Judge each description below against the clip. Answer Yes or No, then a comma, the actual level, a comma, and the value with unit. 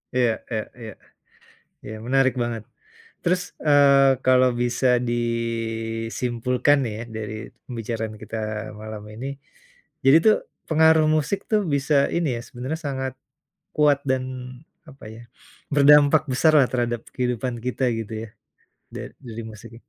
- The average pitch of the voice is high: No, low, 125 Hz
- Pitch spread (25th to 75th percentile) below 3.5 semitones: No, average, 3.8 semitones